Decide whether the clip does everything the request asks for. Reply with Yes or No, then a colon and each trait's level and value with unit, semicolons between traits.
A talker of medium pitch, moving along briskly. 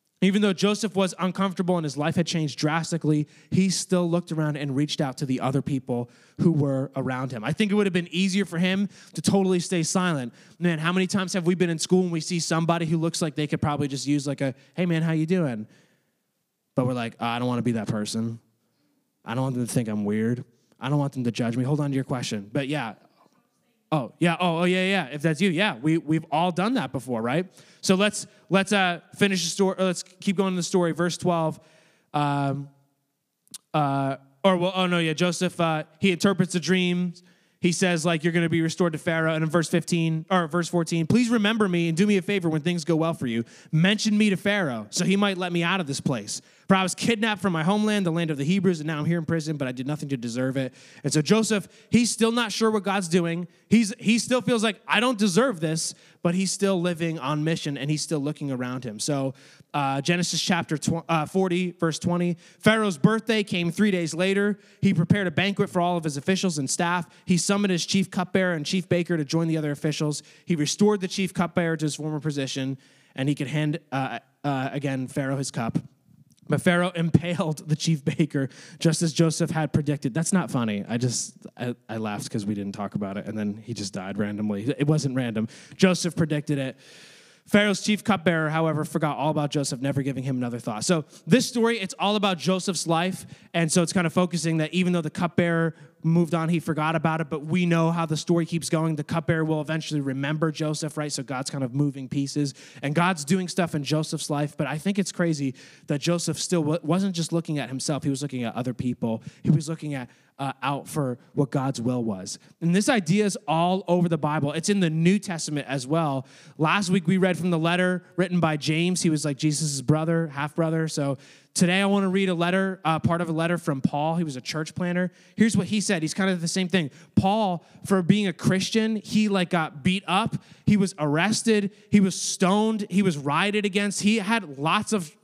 Yes: medium, 165 Hz; fast, 230 wpm